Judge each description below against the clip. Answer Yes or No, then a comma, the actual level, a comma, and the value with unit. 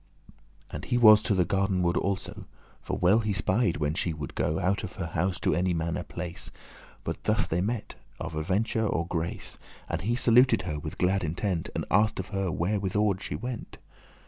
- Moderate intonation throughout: Yes, average, 3.8 semitones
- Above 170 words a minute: Yes, average, 200 wpm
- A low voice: Yes, very low, 95 Hz